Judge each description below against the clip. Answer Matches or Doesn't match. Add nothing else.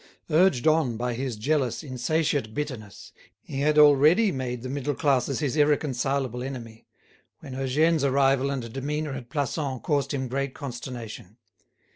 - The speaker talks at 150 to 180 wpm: Doesn't match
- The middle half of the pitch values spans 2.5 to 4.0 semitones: Matches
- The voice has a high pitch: Doesn't match